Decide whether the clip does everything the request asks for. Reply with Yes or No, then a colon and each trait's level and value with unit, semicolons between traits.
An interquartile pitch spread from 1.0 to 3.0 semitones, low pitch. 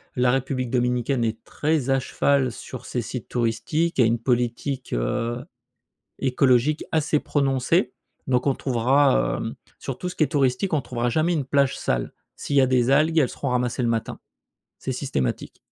Yes: average, 2.7 semitones; low, 130 Hz